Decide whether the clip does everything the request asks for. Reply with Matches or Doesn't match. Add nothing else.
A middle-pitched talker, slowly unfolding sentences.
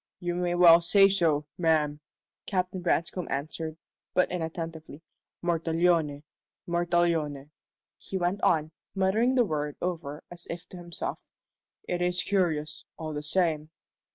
Matches